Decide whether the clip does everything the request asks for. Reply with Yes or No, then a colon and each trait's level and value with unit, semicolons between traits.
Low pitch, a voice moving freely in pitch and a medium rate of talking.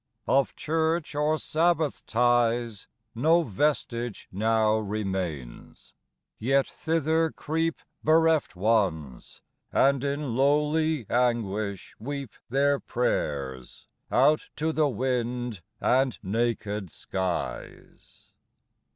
No: low, 125 Hz; wide, 5.9 semitones; slow, 90 wpm